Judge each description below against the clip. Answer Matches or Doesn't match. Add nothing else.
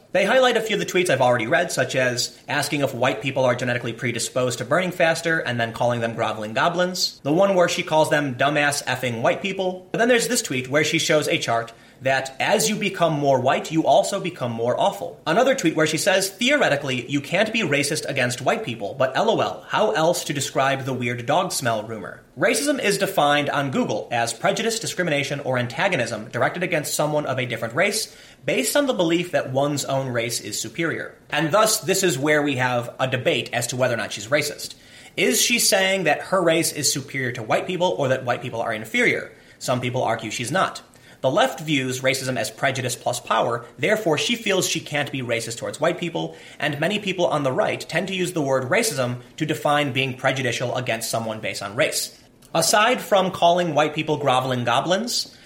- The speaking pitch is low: Doesn't match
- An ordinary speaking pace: Doesn't match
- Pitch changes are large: Matches